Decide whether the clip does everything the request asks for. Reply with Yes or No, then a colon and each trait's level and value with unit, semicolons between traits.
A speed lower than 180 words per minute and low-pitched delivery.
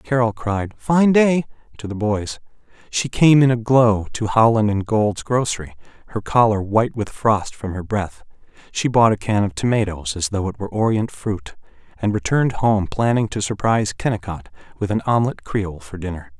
No: average, 185 wpm; low, 110 Hz